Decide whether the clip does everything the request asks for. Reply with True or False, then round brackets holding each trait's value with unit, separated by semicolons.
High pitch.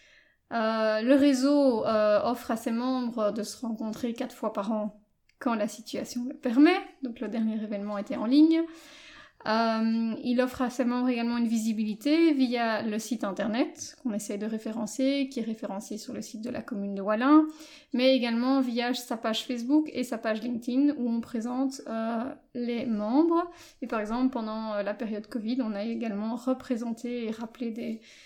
True (240 Hz)